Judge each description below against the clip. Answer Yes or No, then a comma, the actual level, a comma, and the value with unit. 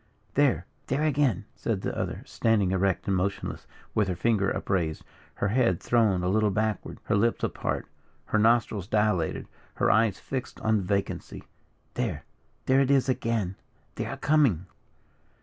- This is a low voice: Yes, low, 105 Hz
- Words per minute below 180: Yes, average, 150 wpm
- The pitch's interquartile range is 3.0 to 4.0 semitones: Yes, average, 3.4 semitones